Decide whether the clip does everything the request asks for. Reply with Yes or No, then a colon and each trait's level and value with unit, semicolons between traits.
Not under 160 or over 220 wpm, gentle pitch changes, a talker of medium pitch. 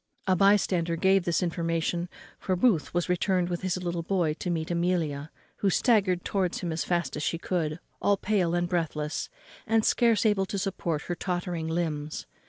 Yes: average, 185 wpm; narrow, 2.3 semitones; medium, 175 Hz